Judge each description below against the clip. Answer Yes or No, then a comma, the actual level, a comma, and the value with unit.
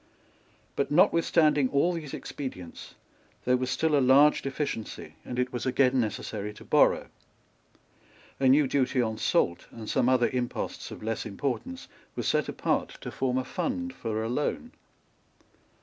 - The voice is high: No, low, 130 Hz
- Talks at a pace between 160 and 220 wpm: No, average, 150 wpm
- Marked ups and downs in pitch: No, average, 4.0 semitones